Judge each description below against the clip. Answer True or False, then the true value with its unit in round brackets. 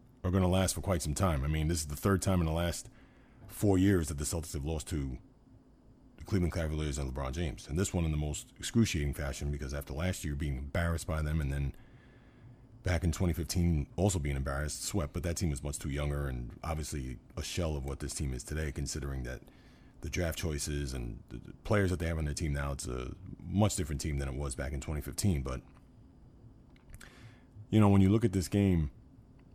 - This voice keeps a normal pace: False (220 wpm)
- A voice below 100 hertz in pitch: True (80 Hz)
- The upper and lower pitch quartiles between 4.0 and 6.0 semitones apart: True (4.9 semitones)